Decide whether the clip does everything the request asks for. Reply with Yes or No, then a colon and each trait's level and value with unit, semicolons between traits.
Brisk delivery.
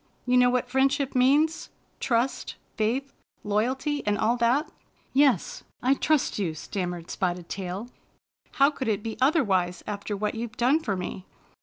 No: average, 155 wpm